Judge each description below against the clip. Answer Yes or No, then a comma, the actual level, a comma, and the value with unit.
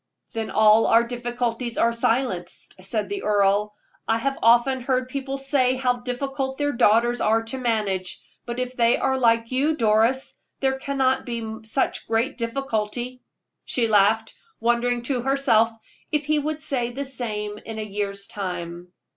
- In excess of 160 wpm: No, average, 155 wpm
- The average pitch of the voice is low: No, high, 240 Hz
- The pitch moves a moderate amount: Yes, average, 3.1 semitones